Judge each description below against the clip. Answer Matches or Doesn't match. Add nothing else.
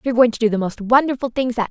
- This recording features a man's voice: Doesn't match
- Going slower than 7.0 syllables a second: Doesn't match